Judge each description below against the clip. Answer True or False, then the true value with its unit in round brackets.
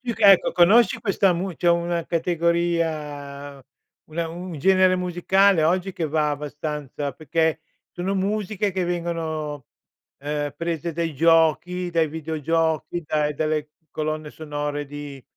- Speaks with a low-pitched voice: False (165 Hz)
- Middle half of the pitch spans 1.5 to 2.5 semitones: False (2.9 semitones)